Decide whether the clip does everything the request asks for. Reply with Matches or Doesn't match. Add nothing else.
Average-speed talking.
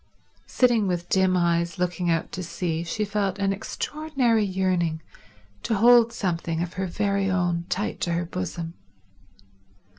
Matches